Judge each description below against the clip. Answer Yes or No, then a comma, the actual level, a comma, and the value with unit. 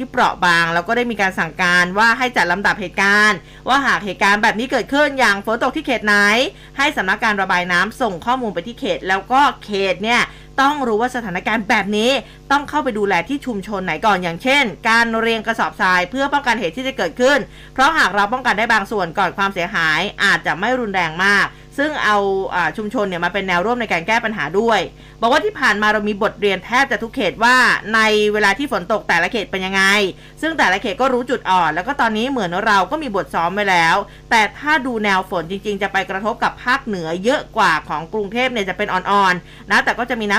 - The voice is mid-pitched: No, high, 215 Hz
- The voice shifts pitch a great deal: No, average, 4.4 semitones